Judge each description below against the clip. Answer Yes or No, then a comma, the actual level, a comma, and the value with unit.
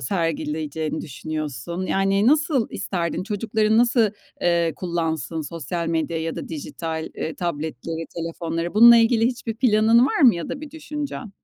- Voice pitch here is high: No, medium, 175 Hz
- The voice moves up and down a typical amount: No, wide, 5.9 semitones